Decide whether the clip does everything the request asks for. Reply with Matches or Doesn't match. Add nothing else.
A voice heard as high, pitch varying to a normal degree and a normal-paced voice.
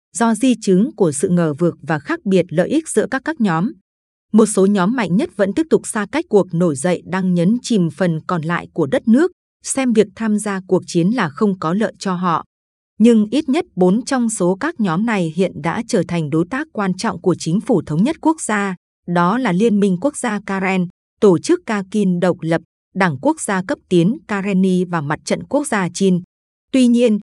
Matches